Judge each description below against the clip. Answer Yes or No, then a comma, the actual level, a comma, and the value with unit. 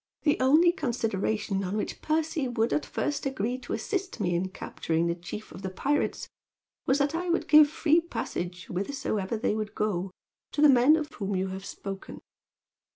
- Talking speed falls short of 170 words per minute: No, average, 180 wpm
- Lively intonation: Yes, wide, 7.4 semitones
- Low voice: No, high, 230 Hz